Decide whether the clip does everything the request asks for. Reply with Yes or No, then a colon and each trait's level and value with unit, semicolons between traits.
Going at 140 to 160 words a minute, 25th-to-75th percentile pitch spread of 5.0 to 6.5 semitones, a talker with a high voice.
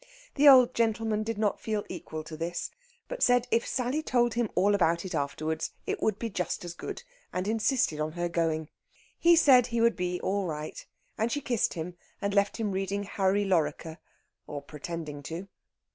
No: average, 190 wpm; wide, 5.6 semitones; high, 195 Hz